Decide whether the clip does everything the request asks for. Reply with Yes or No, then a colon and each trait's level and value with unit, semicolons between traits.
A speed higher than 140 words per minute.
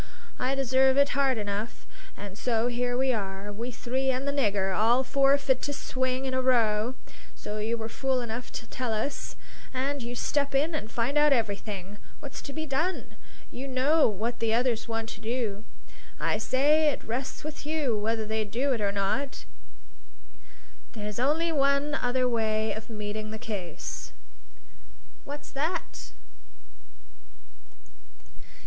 Yes: average, 155 wpm